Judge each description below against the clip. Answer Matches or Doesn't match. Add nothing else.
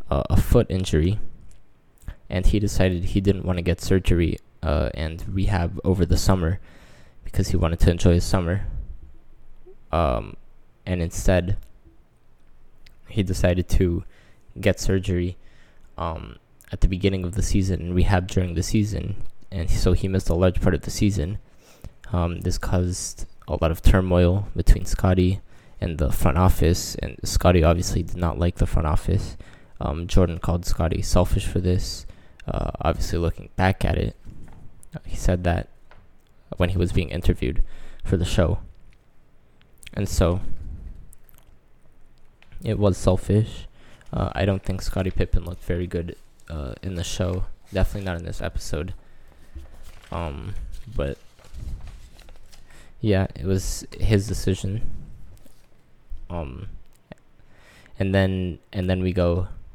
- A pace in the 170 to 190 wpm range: Doesn't match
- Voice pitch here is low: Matches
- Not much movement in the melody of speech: Matches